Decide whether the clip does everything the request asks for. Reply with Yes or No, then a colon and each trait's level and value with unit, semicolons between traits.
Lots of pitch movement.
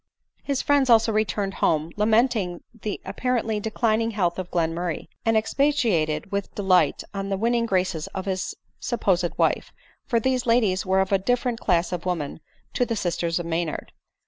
No: average, 4.6 semitones